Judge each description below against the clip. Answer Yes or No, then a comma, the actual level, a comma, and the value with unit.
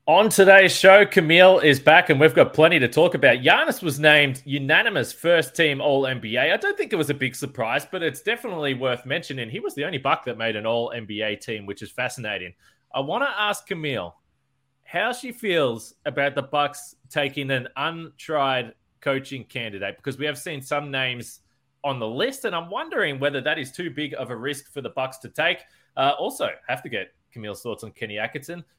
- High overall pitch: No, medium, 140 Hz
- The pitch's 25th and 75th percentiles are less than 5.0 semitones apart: Yes, average, 4.4 semitones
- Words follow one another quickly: Yes, fast, 210 wpm